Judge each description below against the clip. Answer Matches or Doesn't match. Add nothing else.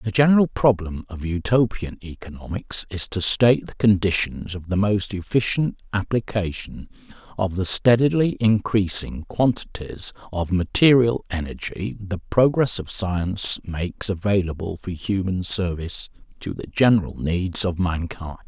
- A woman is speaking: Doesn't match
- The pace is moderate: Doesn't match